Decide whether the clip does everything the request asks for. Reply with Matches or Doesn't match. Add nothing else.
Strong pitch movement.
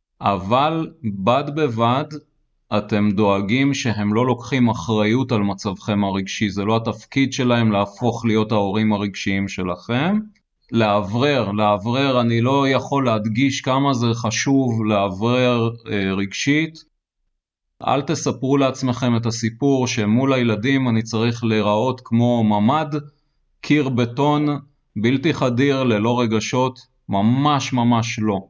Doesn't match